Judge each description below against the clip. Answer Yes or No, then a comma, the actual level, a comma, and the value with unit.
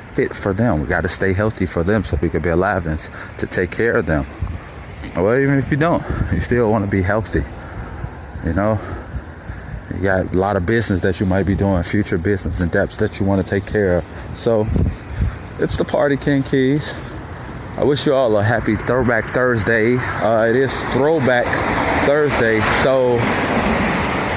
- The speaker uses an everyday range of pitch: Yes, average, 4.0 semitones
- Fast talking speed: No, average, 185 wpm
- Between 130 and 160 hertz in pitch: No, low, 100 Hz